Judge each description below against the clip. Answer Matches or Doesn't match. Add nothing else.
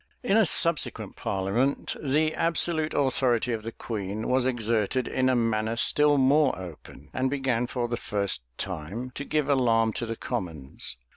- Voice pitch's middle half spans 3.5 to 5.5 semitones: Matches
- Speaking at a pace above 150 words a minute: Matches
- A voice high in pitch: Doesn't match